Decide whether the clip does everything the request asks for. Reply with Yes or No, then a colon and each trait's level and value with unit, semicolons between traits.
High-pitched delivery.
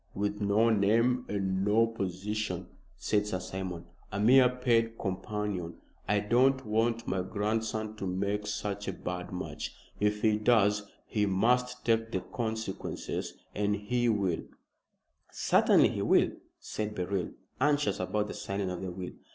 No: low, 105 Hz